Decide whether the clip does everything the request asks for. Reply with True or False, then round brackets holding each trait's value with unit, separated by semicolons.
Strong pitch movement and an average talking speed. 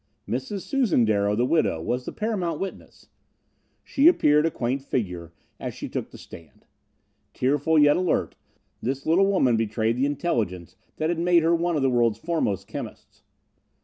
True (7.0 semitones; 165 wpm)